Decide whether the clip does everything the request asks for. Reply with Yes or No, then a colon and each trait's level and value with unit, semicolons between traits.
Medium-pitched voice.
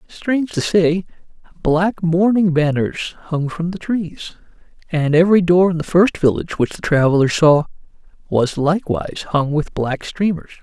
Yes: medium, 165 Hz